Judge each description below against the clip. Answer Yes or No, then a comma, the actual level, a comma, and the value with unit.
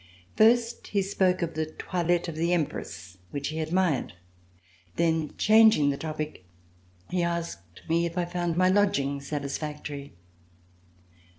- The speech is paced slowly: Yes, slow, 130 wpm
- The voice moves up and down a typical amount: Yes, average, 3.5 semitones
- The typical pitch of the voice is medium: Yes, medium, 165 Hz